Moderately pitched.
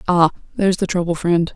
Yes: medium, 175 Hz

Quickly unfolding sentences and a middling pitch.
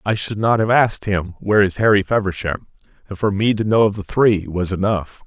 No: fast, 230 wpm; low, 100 Hz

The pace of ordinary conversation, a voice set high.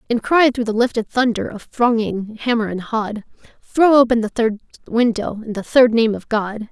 Yes: average, 195 wpm; high, 230 Hz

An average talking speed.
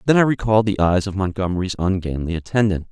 Yes: average, 185 wpm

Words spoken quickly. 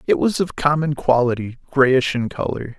No: average, 170 wpm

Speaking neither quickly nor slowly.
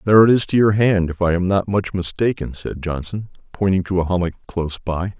No: fast, 230 wpm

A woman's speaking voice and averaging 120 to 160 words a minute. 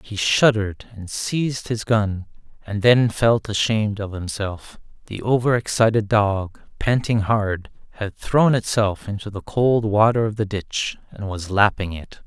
No: male; average, 155 wpm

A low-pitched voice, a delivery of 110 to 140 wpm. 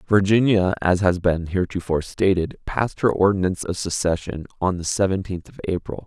No: very low, 95 Hz; average, 160 wpm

